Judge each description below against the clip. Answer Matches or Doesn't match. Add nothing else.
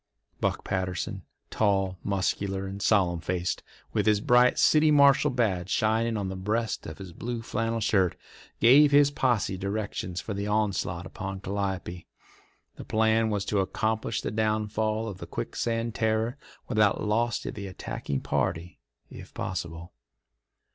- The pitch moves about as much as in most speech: Matches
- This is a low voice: Matches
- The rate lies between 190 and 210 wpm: Doesn't match